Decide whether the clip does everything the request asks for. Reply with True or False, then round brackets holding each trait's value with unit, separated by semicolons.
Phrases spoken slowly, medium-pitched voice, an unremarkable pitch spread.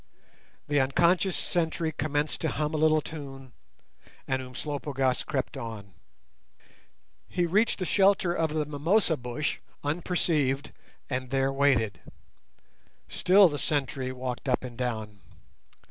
True (120 wpm; 145 Hz; 3.8 semitones)